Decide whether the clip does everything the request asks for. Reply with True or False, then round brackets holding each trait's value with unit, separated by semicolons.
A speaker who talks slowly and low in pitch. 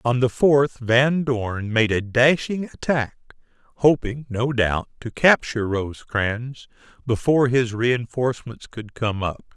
True (130 wpm; 120 Hz)